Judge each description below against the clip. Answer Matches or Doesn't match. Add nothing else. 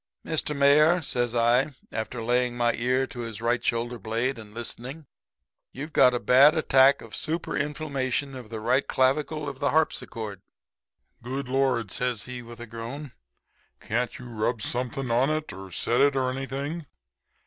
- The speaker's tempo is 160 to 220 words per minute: Matches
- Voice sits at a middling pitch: Doesn't match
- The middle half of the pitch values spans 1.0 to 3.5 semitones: Matches